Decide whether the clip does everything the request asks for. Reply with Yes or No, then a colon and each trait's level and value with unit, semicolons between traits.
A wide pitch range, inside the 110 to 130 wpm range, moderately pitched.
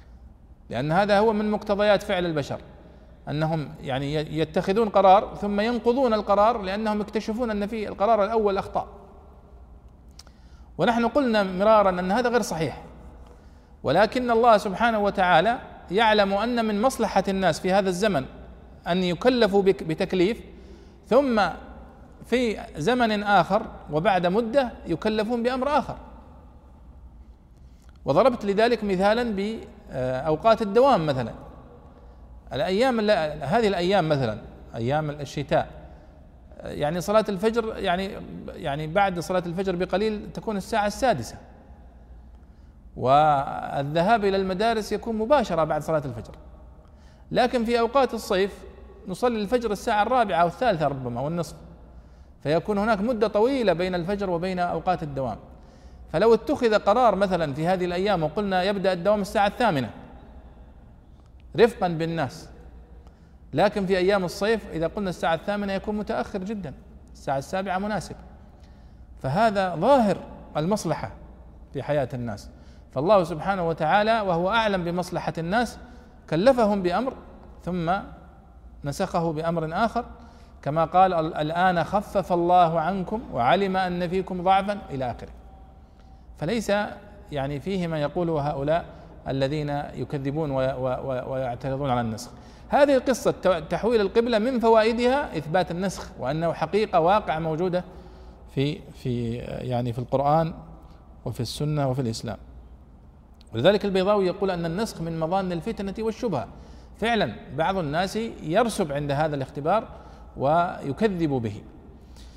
Yes: wide, 9.0 semitones; average, 115 wpm; medium, 175 Hz